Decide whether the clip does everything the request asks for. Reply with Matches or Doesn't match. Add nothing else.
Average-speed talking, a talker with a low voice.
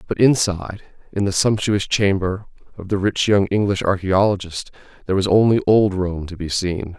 Matches